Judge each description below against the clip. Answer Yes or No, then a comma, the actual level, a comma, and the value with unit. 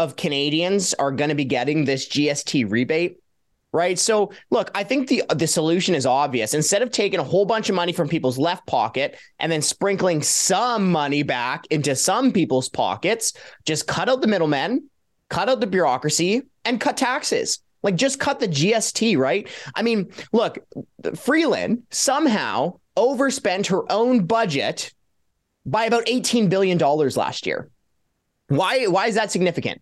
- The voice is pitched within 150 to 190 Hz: Yes, medium, 185 Hz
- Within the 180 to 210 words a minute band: No, average, 165 wpm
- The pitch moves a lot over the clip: Yes, wide, 7.0 semitones